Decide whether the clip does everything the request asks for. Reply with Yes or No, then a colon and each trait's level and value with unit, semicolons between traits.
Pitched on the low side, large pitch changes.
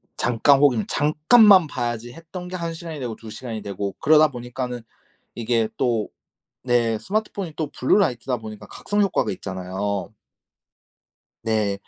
Yes: low, 125 Hz; wide, 6.2 semitones